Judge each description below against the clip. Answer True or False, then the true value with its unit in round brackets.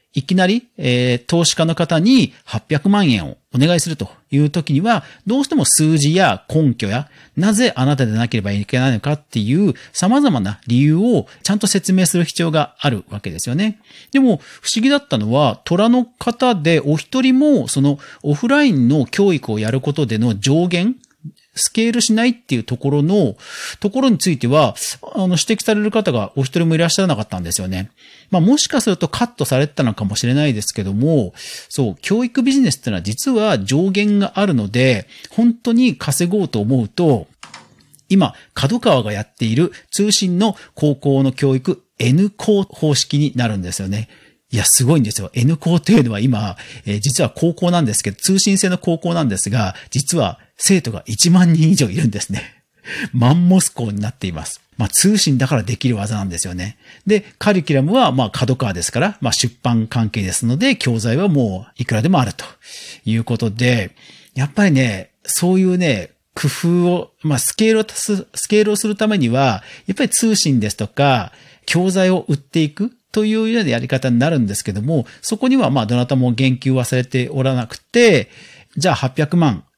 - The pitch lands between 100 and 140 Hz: False (150 Hz)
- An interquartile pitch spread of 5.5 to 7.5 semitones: False (8.1 semitones)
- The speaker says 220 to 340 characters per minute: False (355 characters per minute)